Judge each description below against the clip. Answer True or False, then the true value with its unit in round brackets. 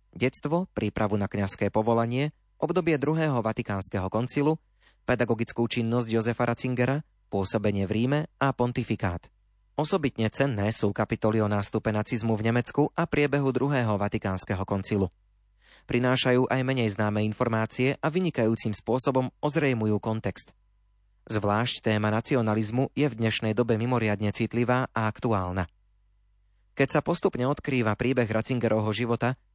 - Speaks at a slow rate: False (120 wpm)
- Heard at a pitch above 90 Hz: True (115 Hz)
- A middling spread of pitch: True (3.6 semitones)